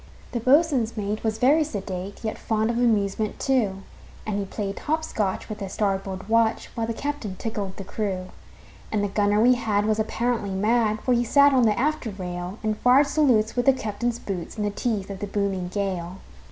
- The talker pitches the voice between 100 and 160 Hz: No, high, 215 Hz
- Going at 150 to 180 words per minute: No, average, 200 wpm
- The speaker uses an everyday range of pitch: Yes, average, 3.3 semitones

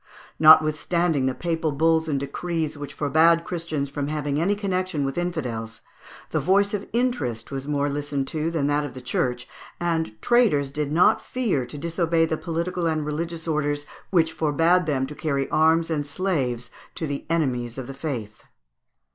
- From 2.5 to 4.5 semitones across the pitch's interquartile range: Yes, average, 3.1 semitones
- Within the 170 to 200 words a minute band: Yes, average, 175 wpm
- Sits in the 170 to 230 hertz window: No, medium, 155 Hz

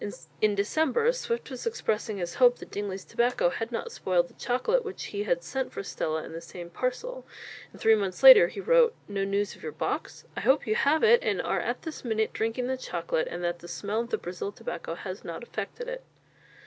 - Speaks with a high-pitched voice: Yes, high, 220 Hz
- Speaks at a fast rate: Yes, fast, 215 wpm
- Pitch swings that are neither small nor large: No, wide, 6.9 semitones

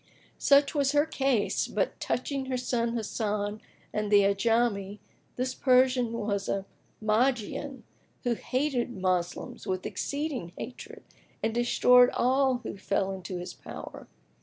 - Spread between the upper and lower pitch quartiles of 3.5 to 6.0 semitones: Yes, average, 4.3 semitones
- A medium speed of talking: No, slow, 130 wpm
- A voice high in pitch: Yes, high, 235 Hz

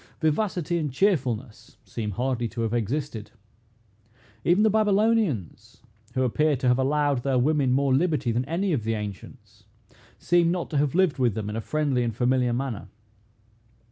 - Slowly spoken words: No, average, 165 wpm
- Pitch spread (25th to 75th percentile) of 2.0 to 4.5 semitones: No, average, 5.2 semitones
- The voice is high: No, low, 135 Hz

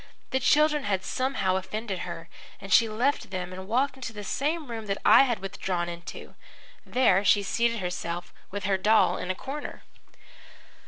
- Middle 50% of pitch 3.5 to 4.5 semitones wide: No, average, 5.1 semitones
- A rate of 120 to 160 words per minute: No, average, 170 wpm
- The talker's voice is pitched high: Yes, high, 205 Hz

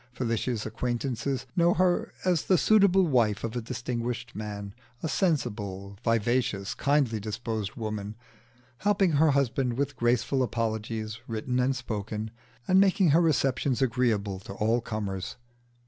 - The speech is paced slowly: Yes, slow, 130 wpm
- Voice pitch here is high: No, low, 120 Hz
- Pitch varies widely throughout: No, average, 4.5 semitones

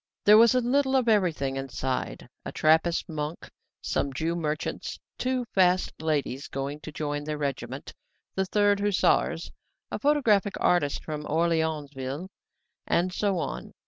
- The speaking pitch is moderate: Yes, medium, 160 Hz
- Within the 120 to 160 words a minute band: Yes, average, 140 wpm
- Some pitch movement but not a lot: No, wide, 5.7 semitones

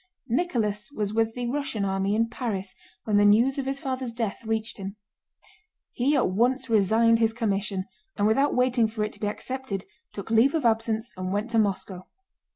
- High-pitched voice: Yes, high, 225 Hz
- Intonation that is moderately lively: Yes, average, 3.3 semitones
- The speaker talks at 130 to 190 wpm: Yes, average, 185 wpm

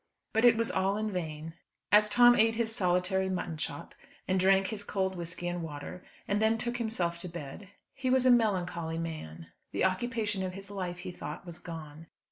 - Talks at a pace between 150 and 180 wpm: No, average, 195 wpm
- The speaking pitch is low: No, high, 190 Hz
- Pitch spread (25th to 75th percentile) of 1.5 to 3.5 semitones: No, average, 4.1 semitones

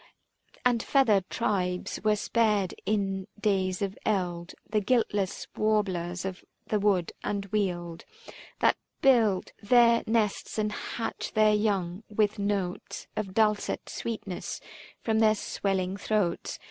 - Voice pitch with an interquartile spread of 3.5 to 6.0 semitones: No, narrow, 2.5 semitones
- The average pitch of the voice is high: Yes, high, 205 Hz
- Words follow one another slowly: Yes, slow, 120 wpm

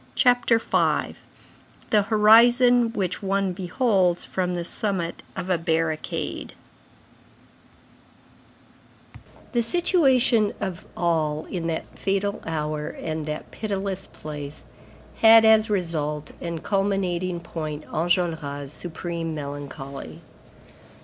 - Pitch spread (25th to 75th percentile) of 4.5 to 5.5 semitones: Yes, average, 4.9 semitones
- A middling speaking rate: No, slow, 95 wpm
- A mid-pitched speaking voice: Yes, medium, 180 Hz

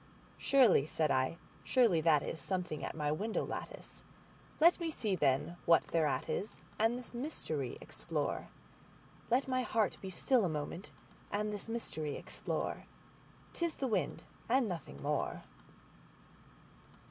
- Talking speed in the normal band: No, slow, 130 wpm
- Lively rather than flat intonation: Yes, wide, 7.7 semitones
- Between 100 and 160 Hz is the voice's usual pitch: No, high, 190 Hz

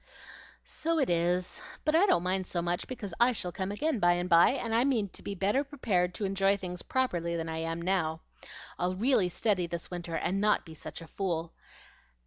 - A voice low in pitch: No, medium, 185 Hz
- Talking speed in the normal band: No, fast, 210 wpm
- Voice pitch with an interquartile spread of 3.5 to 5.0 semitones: Yes, average, 4.4 semitones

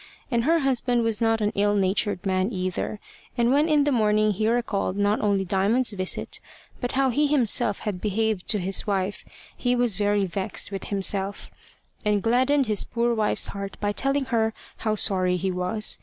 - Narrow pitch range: No, average, 3.4 semitones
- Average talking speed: Yes, average, 185 wpm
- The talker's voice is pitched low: No, high, 210 Hz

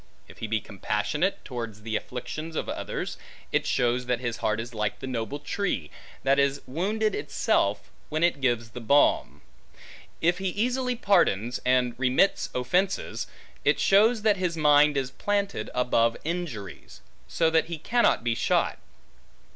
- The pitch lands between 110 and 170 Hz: Yes, medium, 140 Hz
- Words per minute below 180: Yes, average, 155 wpm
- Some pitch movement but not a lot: No, wide, 7.2 semitones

